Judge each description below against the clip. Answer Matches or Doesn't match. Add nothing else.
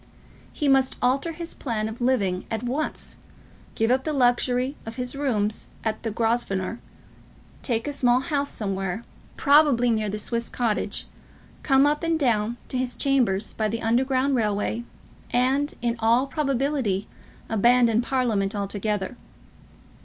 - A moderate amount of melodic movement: Matches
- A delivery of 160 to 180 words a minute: Doesn't match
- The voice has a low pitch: Doesn't match